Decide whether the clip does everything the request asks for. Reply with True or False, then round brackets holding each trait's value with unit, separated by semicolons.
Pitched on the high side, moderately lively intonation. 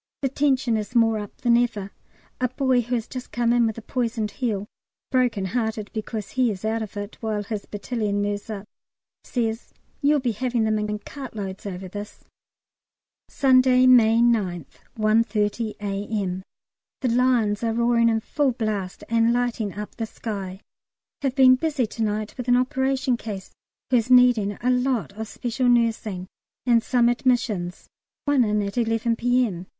True (230 Hz; 3.0 semitones)